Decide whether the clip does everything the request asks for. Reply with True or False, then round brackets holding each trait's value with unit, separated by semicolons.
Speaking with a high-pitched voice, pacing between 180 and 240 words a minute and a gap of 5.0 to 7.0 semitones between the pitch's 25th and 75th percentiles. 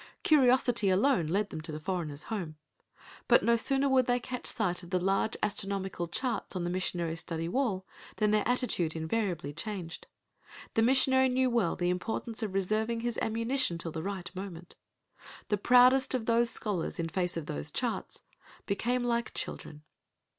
False (200 Hz; 170 wpm; 5.5 semitones)